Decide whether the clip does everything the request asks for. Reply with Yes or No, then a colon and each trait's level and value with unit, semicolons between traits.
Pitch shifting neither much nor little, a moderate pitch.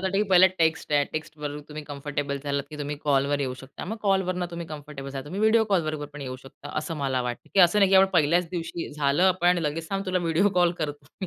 Yes: average, 3.7 semitones; medium, 155 Hz